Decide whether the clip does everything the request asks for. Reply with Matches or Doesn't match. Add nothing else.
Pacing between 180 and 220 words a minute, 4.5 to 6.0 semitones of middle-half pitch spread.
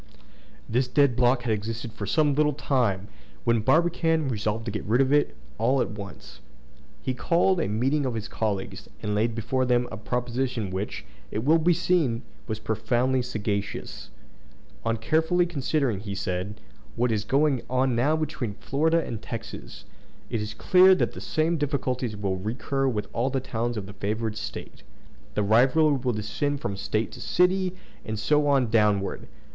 Doesn't match